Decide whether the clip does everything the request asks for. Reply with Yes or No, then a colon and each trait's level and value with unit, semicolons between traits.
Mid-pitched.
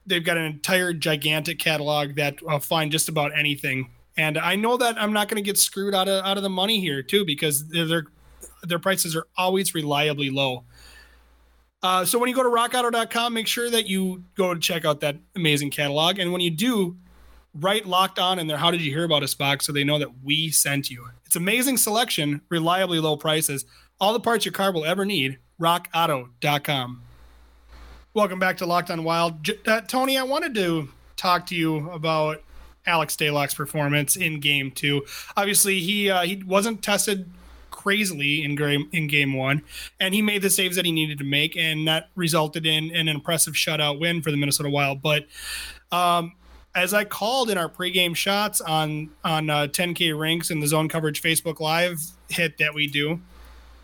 Yes: medium, 165 Hz